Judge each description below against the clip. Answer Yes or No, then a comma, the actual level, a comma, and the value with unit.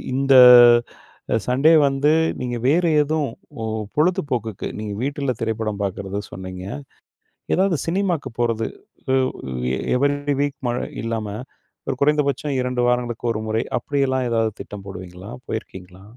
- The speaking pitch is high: No, low, 125 Hz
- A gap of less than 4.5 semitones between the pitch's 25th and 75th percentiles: No, average, 4.8 semitones